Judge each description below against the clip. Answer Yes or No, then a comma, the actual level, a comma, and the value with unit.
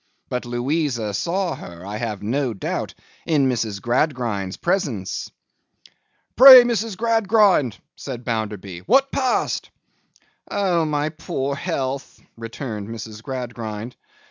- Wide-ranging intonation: Yes, wide, 7.3 semitones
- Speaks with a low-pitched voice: Yes, low, 130 Hz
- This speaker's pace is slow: Yes, slow, 110 wpm